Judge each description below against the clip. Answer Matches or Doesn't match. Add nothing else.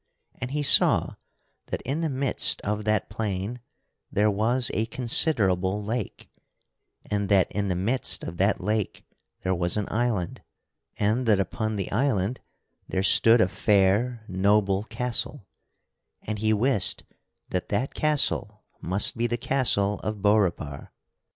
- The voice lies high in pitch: Doesn't match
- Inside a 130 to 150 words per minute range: Matches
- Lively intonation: Doesn't match